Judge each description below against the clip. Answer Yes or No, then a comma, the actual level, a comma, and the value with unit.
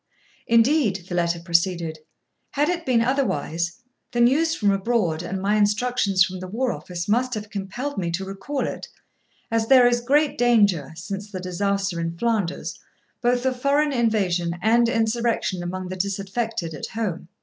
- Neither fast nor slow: Yes, average, 160 wpm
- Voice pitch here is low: No, high, 205 Hz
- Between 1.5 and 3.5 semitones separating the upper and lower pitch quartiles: No, average, 4.9 semitones